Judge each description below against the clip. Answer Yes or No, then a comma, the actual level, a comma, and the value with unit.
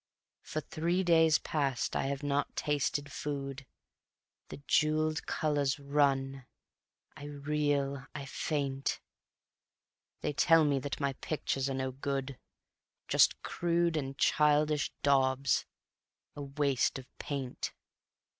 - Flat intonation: Yes, narrow, 1.8 semitones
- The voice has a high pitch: No, medium, 140 Hz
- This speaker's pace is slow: Yes, slow, 115 wpm